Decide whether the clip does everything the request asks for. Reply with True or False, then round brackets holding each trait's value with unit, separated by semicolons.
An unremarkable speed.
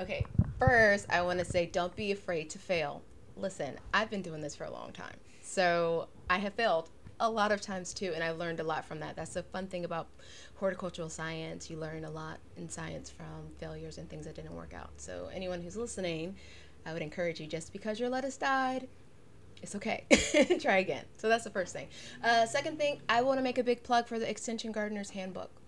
False (215 wpm)